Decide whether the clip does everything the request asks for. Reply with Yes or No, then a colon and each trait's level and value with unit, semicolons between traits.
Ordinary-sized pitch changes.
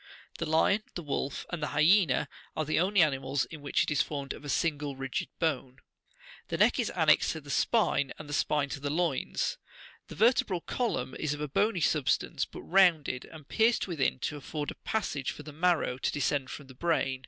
Yes: average, 3.4 semitones